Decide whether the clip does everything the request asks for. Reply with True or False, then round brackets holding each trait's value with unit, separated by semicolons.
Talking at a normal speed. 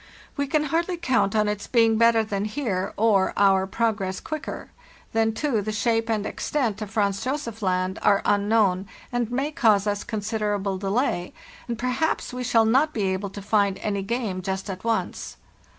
True (180 wpm)